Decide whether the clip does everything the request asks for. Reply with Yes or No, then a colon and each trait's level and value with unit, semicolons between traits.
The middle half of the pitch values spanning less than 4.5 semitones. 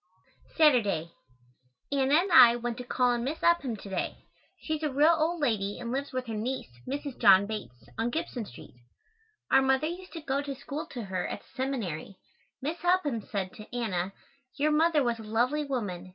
No: wide, 5.6 semitones